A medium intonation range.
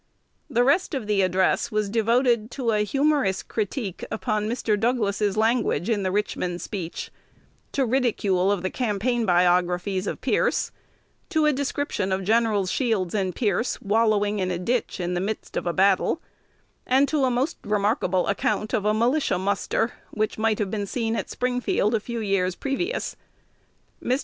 Yes: average, 3.9 semitones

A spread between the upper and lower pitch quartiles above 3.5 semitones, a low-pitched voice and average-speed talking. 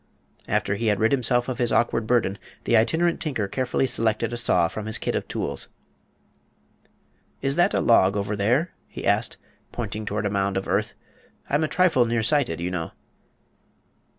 Yes: average, 3.9 semitones; low, 115 Hz; average, 175 wpm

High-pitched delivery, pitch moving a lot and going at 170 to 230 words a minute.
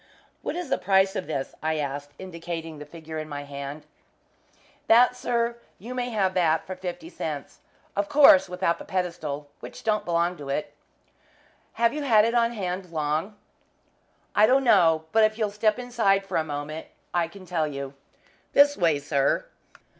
No: medium, 180 Hz; wide, 6.1 semitones; average, 175 wpm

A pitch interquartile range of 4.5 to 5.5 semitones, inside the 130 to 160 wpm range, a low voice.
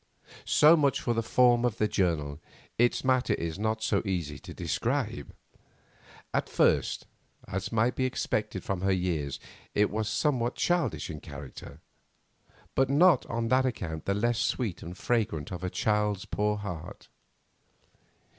Yes: average, 5.2 semitones; average, 150 wpm; low, 105 Hz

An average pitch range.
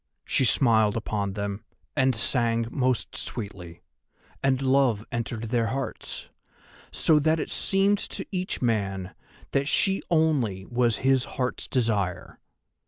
Yes: average, 4.3 semitones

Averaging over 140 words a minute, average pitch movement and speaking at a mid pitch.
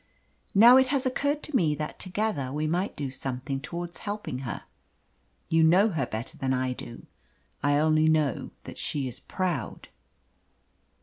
No: average, 160 wpm; wide, 6.4 semitones; medium, 155 Hz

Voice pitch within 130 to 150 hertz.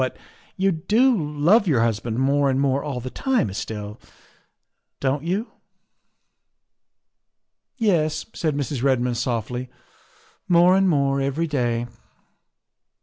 Yes: medium, 140 Hz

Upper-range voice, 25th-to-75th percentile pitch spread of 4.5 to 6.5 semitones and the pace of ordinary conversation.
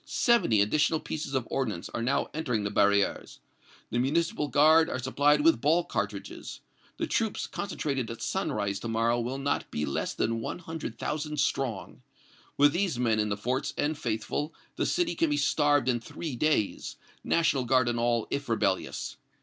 No: low, 135 Hz; average, 5.0 semitones; average, 175 wpm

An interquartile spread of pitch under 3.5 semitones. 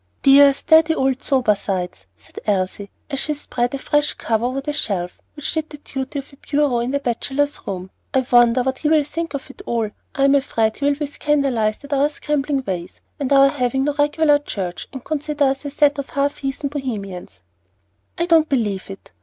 No: average, 3.9 semitones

